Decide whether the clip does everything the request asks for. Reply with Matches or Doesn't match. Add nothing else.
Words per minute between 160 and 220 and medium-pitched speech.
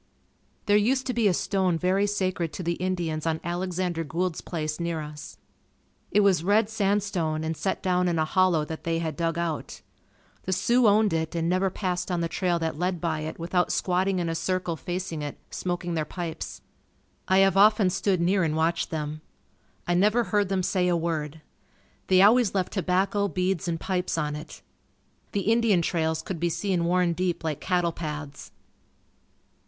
Matches